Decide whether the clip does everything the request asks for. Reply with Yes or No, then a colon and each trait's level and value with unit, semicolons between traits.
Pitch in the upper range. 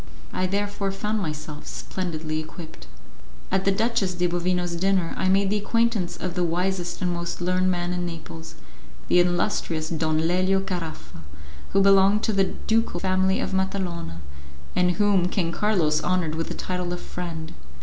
No: medium, 180 Hz